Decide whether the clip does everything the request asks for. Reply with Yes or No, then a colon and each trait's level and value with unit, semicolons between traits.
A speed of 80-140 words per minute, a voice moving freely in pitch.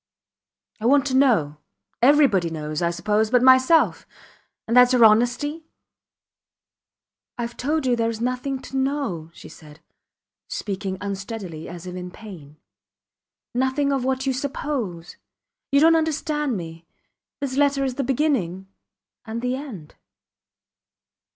Yes: slow, 135 wpm; wide, 6.6 semitones